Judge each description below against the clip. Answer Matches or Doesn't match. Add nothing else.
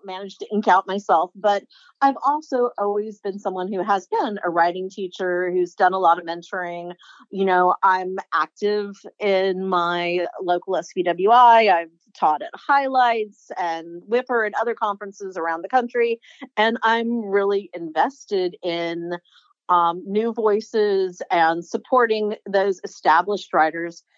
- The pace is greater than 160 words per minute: Doesn't match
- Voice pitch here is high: Matches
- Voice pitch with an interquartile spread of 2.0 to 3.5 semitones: Doesn't match